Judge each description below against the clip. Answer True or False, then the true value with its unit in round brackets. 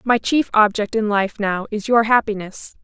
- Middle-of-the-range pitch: False (215 Hz)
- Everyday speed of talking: True (190 wpm)